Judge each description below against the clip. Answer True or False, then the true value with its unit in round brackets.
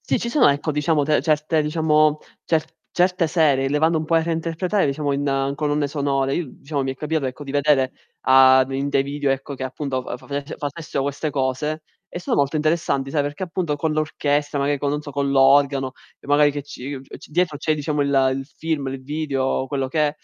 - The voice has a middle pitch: True (145 Hz)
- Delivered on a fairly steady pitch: True (2.1 semitones)